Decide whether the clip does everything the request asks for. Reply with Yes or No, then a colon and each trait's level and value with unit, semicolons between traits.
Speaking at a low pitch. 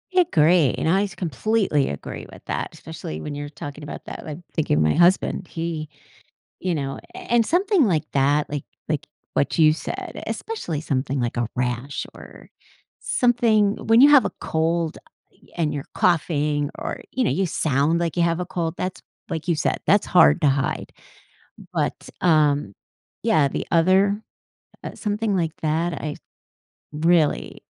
No: medium, 160 Hz